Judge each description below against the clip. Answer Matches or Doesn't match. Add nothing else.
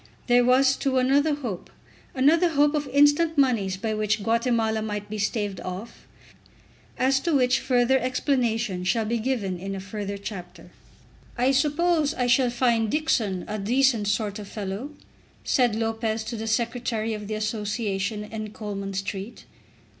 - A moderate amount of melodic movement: Matches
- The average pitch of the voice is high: Matches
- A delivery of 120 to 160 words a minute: Matches